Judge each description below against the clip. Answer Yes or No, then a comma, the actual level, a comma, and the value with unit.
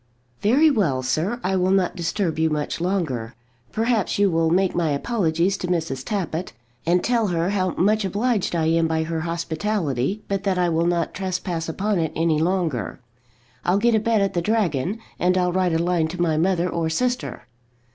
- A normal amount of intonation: Yes, average, 3.5 semitones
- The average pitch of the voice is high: No, medium, 180 Hz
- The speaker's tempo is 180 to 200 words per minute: Yes, average, 190 wpm